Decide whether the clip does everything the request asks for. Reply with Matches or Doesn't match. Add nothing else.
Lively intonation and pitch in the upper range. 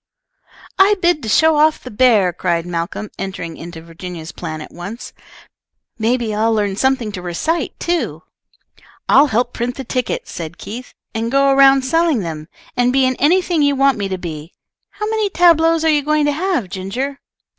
Matches